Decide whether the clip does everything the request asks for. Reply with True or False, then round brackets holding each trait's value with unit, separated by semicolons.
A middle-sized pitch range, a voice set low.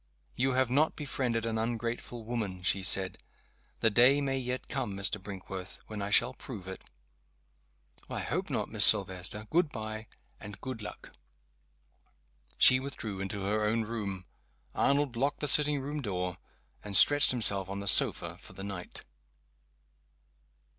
True (4.7 semitones; 110 Hz)